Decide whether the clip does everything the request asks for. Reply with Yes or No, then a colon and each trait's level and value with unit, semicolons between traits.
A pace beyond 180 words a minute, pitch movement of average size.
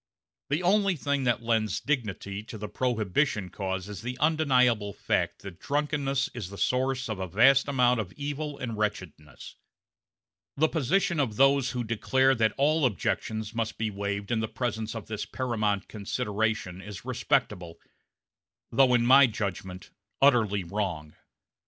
No: average, 150 wpm; average, 4.9 semitones